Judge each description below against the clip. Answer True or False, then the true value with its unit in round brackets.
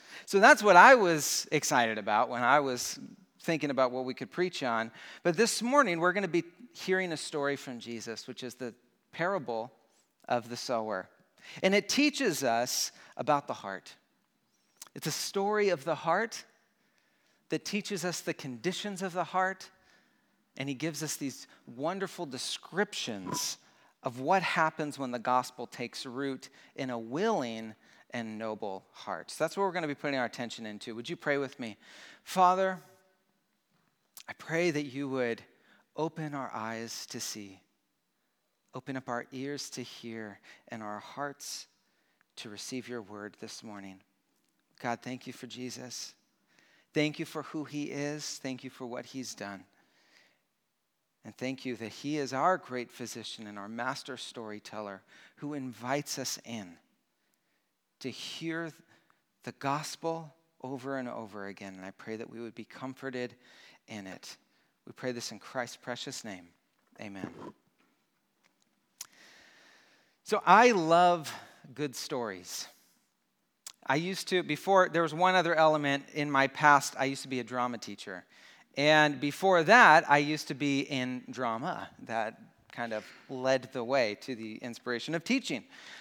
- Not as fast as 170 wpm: True (155 wpm)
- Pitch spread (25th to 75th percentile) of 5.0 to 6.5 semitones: True (5.6 semitones)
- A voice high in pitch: False (135 Hz)